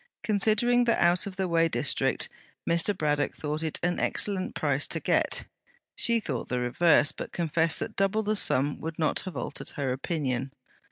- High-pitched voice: No, medium, 170 Hz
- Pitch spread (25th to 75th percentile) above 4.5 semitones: Yes, average, 5.0 semitones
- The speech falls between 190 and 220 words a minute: No, average, 175 wpm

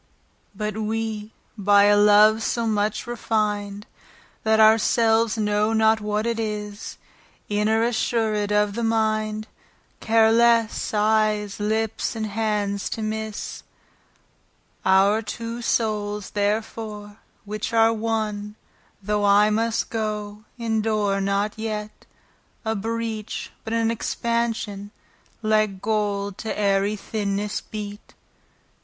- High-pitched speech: Yes, high, 215 Hz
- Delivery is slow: Yes, slow, 110 wpm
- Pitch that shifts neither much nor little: No, narrow, 1.3 semitones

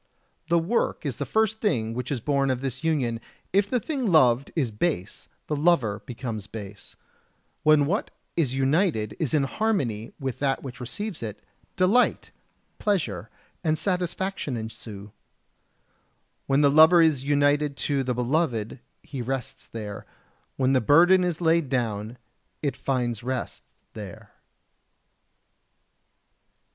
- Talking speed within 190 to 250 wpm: No, slow, 135 wpm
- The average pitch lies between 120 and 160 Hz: Yes, low, 135 Hz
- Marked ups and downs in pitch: Yes, wide, 5.8 semitones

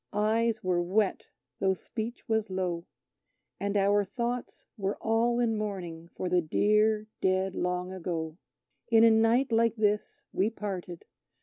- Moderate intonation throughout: Yes, average, 3.4 semitones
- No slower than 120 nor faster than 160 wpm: Yes, average, 140 wpm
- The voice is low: No, high, 205 Hz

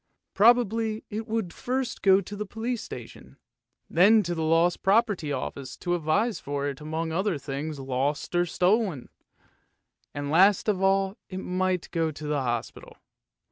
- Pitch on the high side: No, medium, 180 Hz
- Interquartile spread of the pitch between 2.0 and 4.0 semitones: No, wide, 5.5 semitones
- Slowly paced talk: No, average, 155 wpm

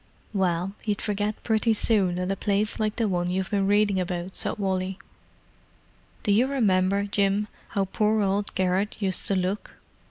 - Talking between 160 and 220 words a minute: Yes, average, 170 wpm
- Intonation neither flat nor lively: No, narrow, 2.0 semitones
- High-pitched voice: Yes, high, 200 Hz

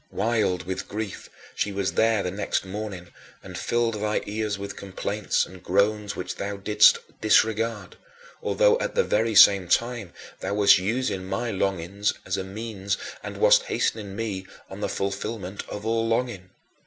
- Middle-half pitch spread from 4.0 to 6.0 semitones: No, narrow, 2.6 semitones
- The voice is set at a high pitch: No, low, 105 Hz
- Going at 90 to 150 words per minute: No, average, 165 wpm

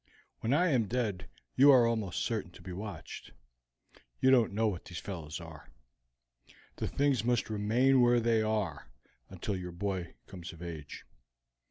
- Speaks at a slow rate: No, average, 160 wpm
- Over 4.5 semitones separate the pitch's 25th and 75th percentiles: Yes, average, 5.2 semitones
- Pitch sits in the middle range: No, low, 105 Hz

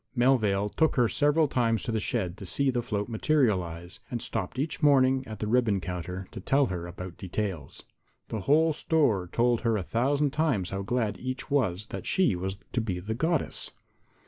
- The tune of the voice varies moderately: No, wide, 5.8 semitones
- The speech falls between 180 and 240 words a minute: Yes, average, 190 wpm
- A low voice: Yes, low, 115 Hz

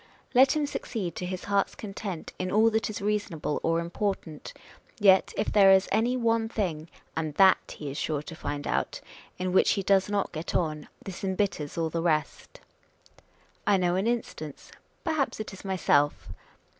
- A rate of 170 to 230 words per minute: Yes, average, 175 wpm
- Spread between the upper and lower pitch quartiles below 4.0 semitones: No, average, 4.4 semitones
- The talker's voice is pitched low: No, high, 190 Hz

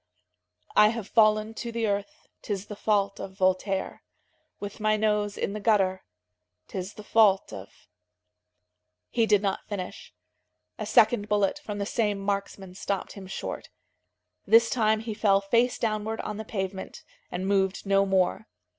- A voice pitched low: No, high, 205 Hz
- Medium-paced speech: Yes, average, 160 wpm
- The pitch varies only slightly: Yes, narrow, 2.0 semitones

